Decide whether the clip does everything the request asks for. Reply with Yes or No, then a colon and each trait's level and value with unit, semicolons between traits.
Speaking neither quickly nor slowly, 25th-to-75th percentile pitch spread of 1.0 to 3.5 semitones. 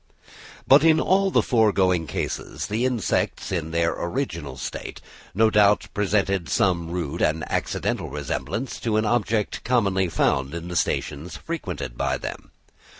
No: average, 145 wpm; average, 5.2 semitones